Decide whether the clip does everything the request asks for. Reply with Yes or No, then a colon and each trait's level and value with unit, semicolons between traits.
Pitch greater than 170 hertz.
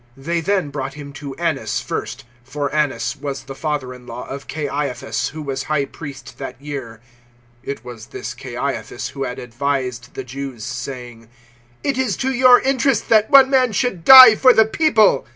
No: medium, 140 Hz